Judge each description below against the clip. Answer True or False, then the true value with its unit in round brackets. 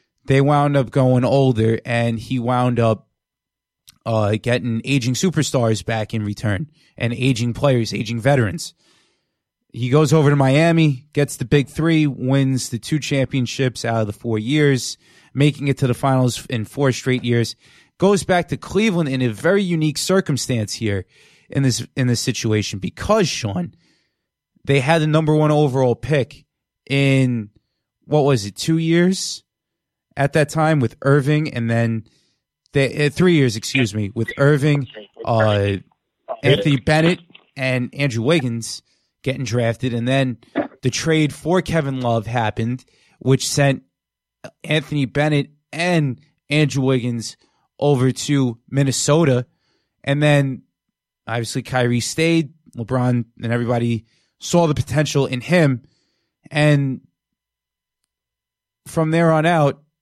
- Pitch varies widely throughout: False (4.1 semitones)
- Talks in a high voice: False (135 Hz)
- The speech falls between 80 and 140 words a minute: True (135 wpm)